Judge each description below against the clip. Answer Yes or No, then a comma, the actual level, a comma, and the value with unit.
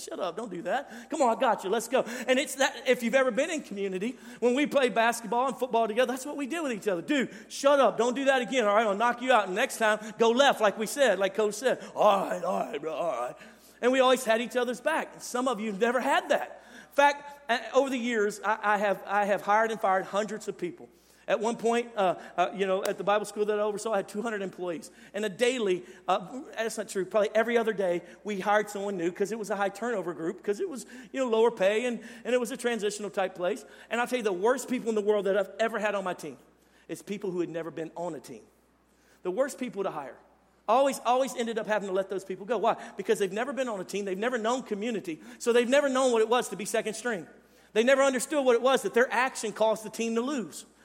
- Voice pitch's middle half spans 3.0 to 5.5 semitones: Yes, average, 3.7 semitones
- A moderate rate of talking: No, fast, 270 wpm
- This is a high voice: Yes, high, 225 Hz